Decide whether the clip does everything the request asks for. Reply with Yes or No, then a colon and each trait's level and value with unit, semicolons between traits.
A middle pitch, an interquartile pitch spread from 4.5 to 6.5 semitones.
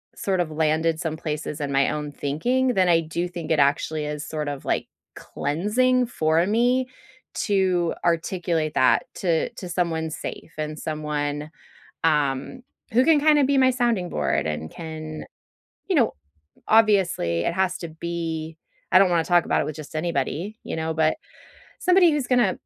Yes: medium, 165 Hz; average, 4.9 semitones